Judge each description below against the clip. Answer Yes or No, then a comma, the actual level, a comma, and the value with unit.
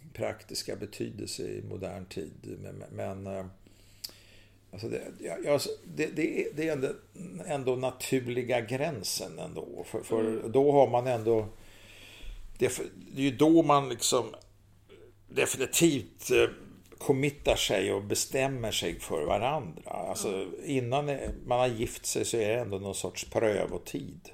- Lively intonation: Yes, wide, 5.7 semitones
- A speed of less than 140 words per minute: Yes, average, 130 wpm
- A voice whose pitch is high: No, low, 115 Hz